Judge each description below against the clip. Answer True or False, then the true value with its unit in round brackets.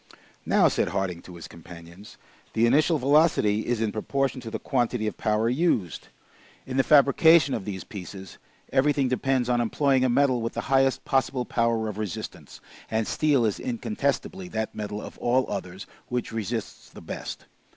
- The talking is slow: False (170 wpm)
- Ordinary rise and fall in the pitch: True (4.3 semitones)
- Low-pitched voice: True (120 Hz)